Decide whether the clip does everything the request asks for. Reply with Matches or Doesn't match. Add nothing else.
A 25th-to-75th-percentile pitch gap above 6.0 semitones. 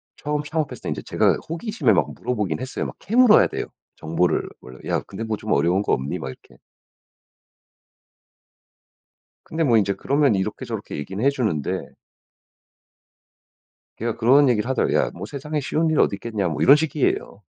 Matches